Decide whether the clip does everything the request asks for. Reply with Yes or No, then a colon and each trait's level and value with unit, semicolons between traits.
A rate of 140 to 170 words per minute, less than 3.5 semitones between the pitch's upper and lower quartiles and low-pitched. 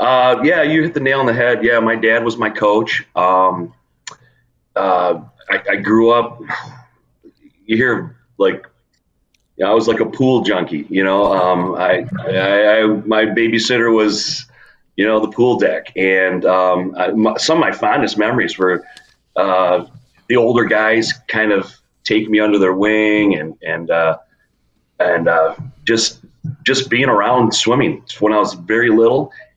No: average, 165 wpm; average, 4.3 semitones; low, 110 Hz